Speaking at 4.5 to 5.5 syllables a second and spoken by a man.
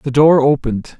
Yes: 5.3 syllables/s; male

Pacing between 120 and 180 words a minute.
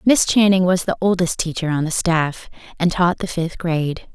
No: fast, 205 wpm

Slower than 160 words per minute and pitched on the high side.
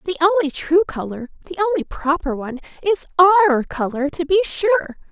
Yes: average, 140 wpm; very high, 330 Hz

